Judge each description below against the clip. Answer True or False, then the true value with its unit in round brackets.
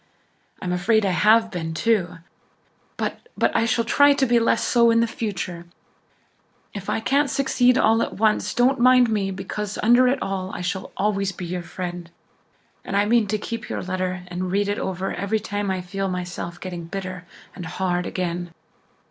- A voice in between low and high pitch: False (195 Hz)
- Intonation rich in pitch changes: False (4.0 semitones)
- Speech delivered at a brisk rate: False (180 wpm)